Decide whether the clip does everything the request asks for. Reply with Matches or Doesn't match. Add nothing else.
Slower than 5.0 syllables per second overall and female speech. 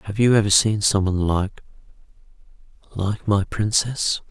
Doesn't match